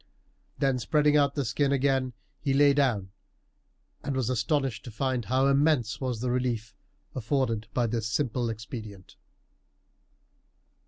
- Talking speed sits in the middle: No, slow, 130 wpm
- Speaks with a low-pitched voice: Yes, low, 130 Hz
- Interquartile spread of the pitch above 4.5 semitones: No, average, 3.5 semitones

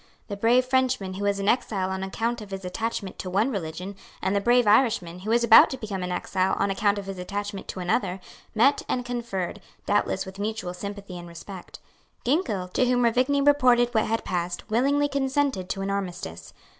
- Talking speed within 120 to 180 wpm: No, average, 195 wpm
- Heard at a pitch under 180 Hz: No, high, 205 Hz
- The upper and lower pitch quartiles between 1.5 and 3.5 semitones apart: No, average, 4.2 semitones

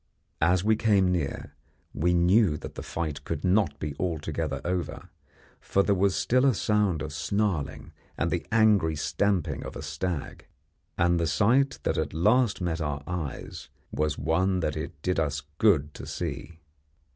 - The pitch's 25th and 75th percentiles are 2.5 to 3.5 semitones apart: No, average, 4.6 semitones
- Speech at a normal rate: Yes, average, 165 wpm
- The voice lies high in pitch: No, very low, 85 Hz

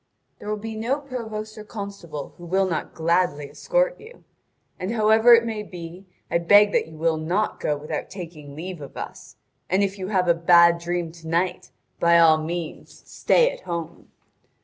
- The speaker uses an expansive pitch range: No, average, 4.2 semitones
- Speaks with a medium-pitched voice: Yes, medium, 180 Hz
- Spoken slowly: No, average, 185 wpm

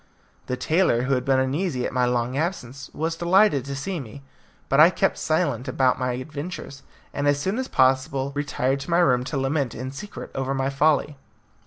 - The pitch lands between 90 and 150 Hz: Yes, medium, 140 Hz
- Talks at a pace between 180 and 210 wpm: Yes, average, 195 wpm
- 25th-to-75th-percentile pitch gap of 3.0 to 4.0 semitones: Yes, average, 3.4 semitones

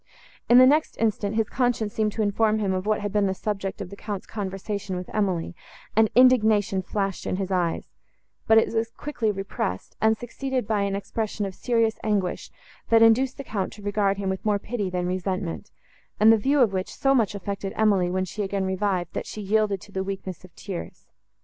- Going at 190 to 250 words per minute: Yes, fast, 205 wpm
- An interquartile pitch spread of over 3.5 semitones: No, narrow, 2.5 semitones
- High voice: Yes, high, 205 Hz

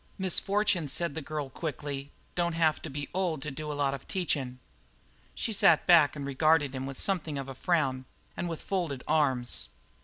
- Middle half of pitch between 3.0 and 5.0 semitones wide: Yes, average, 3.8 semitones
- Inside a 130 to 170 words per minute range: No, average, 185 wpm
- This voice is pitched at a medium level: Yes, medium, 150 Hz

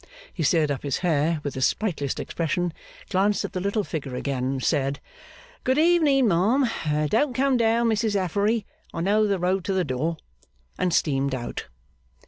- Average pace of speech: Yes, average, 170 wpm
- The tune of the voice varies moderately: No, wide, 6.7 semitones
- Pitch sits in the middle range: Yes, medium, 180 Hz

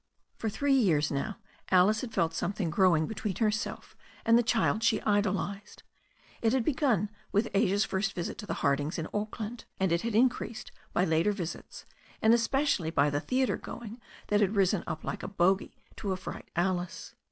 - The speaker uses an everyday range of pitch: Yes, average, 4.1 semitones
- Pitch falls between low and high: No, high, 205 Hz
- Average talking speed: Yes, average, 185 wpm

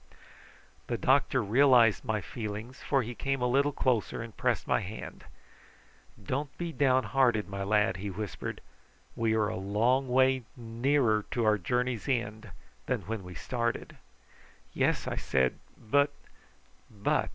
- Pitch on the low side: Yes, low, 115 Hz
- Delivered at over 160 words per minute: No, average, 145 wpm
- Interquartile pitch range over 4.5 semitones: No, average, 3.7 semitones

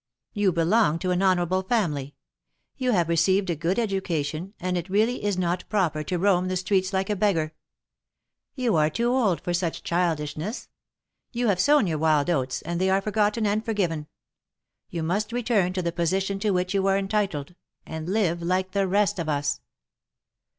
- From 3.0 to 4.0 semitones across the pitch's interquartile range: Yes, average, 3.4 semitones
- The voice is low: No, medium, 185 Hz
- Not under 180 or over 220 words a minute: Yes, average, 185 wpm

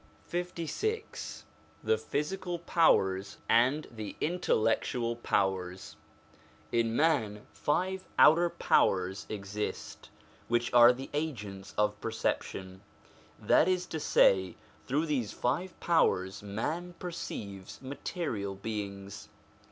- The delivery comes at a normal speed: No, slow, 95 wpm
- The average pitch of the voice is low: Yes, low, 120 Hz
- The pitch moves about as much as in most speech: No, wide, 8.5 semitones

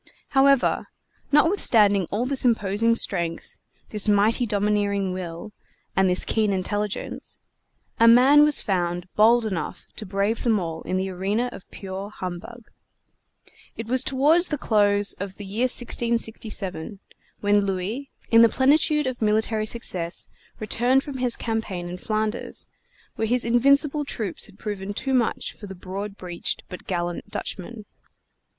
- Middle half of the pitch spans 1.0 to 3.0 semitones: No, average, 3.9 semitones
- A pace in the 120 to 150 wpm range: Yes, average, 145 wpm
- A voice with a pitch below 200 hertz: No, high, 210 Hz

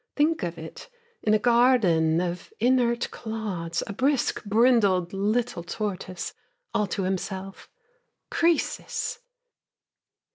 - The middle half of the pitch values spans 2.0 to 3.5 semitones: No, average, 5.0 semitones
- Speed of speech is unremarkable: No, slow, 105 wpm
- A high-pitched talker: Yes, high, 210 Hz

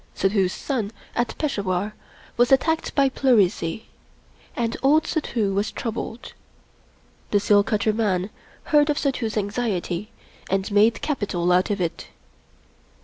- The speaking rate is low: Yes, slow, 125 wpm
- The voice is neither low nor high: No, high, 215 Hz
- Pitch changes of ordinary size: Yes, average, 4.0 semitones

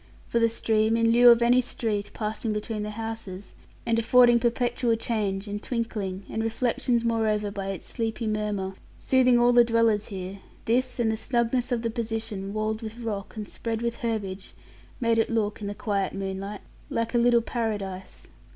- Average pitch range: No, narrow, 2.2 semitones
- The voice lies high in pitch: Yes, high, 225 Hz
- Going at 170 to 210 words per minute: Yes, average, 180 wpm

